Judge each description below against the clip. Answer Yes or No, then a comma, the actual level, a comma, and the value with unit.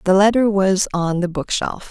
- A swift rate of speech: No, average, 190 wpm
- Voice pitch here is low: No, high, 190 Hz